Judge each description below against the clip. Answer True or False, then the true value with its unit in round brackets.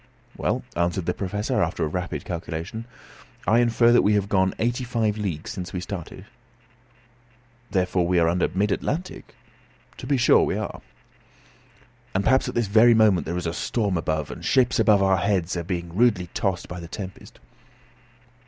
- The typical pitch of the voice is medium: False (95 Hz)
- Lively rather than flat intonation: False (4.1 semitones)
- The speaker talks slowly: False (175 wpm)